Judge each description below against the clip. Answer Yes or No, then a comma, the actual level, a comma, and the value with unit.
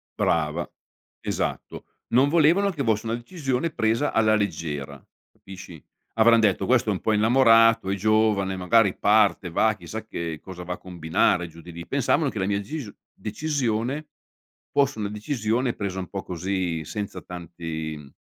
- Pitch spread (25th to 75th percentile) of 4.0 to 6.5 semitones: Yes, average, 4.6 semitones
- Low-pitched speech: Yes, low, 105 Hz